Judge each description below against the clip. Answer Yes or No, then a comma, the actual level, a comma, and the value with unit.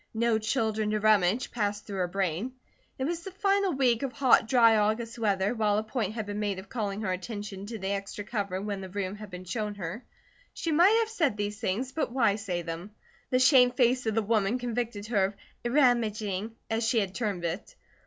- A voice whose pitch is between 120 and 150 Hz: No, high, 215 Hz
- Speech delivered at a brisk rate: Yes, fast, 215 wpm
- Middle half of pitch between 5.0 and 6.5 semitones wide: No, average, 3.4 semitones